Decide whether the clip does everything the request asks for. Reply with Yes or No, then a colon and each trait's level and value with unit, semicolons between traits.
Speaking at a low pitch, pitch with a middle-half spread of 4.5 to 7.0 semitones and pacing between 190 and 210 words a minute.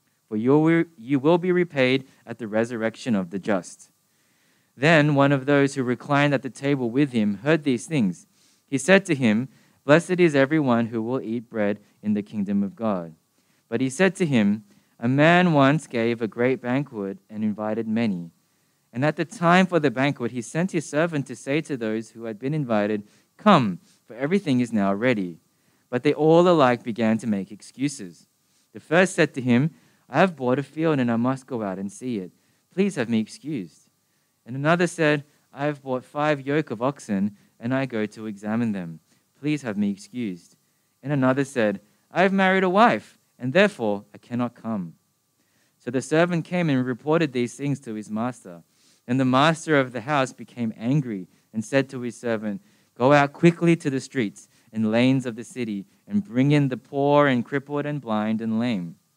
Yes: low, 130 Hz; average, 5.2 semitones; average, 195 wpm